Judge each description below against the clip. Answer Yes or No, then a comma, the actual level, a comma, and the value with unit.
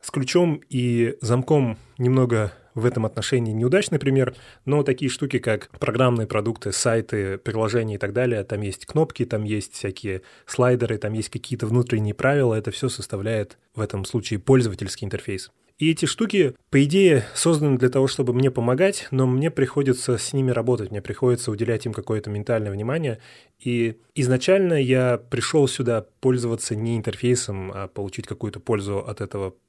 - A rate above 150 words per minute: Yes, fast, 160 wpm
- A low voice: Yes, low, 120 Hz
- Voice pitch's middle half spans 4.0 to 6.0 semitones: No, average, 3.4 semitones